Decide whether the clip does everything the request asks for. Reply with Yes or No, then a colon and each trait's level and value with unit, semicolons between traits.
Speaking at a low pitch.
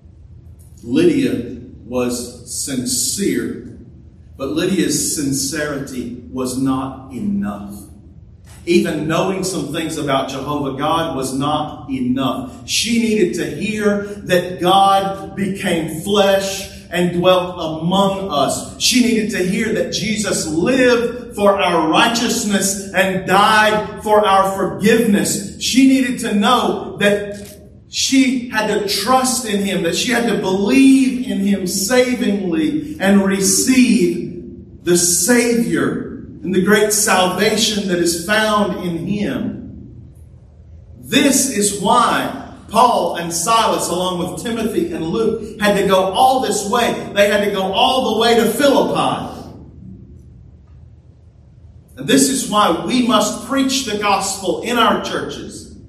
No: high, 195 Hz